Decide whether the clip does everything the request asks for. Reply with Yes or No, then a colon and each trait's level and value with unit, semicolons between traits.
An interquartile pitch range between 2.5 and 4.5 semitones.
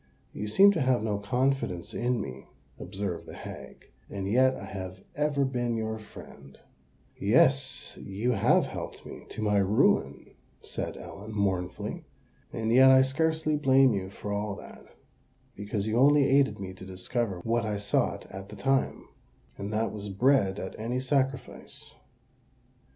No: average, 4.9 semitones